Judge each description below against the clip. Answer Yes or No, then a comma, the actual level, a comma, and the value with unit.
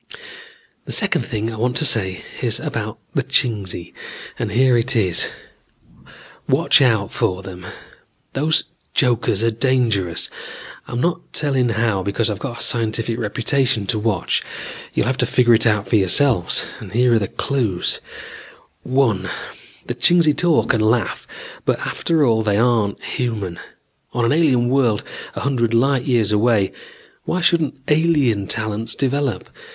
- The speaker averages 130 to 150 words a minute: Yes, average, 145 wpm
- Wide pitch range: No, average, 3.9 semitones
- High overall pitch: No, low, 115 Hz